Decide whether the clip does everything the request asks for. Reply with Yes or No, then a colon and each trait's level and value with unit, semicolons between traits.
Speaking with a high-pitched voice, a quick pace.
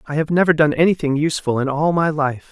No: medium, 150 Hz; fast, 240 wpm